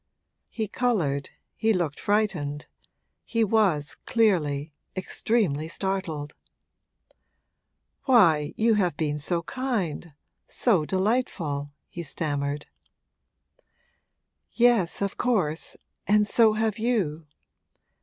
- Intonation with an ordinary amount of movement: No, wide, 6.7 semitones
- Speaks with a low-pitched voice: No, medium, 185 Hz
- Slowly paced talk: Yes, slow, 90 wpm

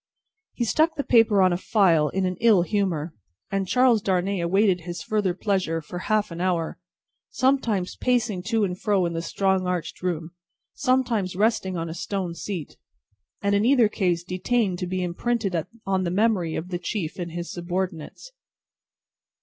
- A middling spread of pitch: Yes, average, 3.6 semitones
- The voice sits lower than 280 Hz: Yes, medium, 185 Hz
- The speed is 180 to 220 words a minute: No, average, 165 wpm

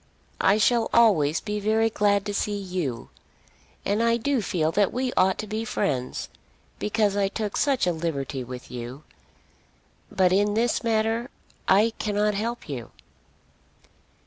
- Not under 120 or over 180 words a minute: Yes, average, 145 wpm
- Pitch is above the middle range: Yes, high, 205 Hz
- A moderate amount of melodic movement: Yes, average, 4.6 semitones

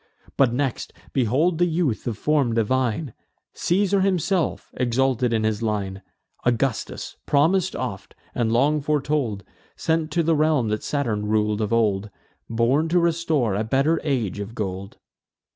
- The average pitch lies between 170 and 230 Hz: No, low, 130 Hz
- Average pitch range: No, wide, 6.0 semitones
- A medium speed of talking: Yes, average, 145 wpm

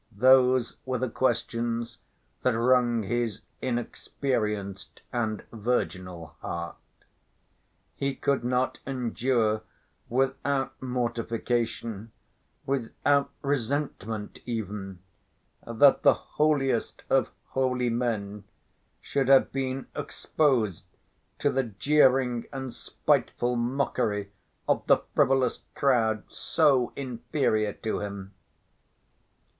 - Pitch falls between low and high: No, low, 120 Hz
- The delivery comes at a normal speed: No, slow, 90 wpm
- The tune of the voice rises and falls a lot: No, average, 3.3 semitones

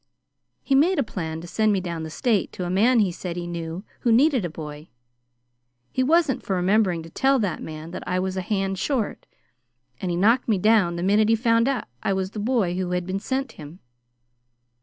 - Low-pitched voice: No, high, 195 Hz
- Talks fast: Yes, fast, 215 wpm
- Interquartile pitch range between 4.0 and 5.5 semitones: Yes, average, 4.7 semitones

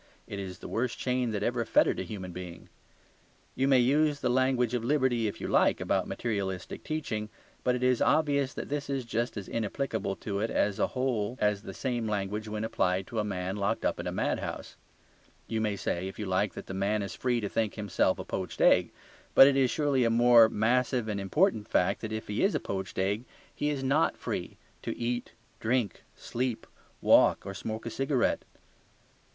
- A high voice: No, low, 115 Hz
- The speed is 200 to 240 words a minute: Yes, fast, 205 wpm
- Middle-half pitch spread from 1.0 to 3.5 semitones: No, average, 3.9 semitones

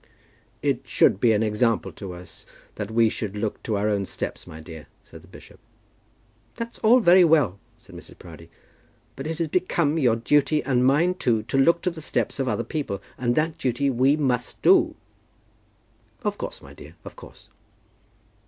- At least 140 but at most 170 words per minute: No, average, 180 wpm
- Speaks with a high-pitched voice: No, low, 125 Hz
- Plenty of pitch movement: Yes, wide, 6.4 semitones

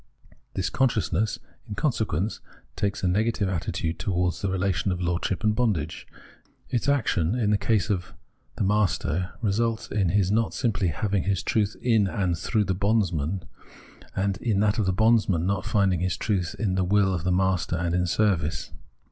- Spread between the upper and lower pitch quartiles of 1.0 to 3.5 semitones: Yes, average, 3.0 semitones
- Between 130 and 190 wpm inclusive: Yes, average, 180 wpm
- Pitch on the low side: Yes, low, 100 Hz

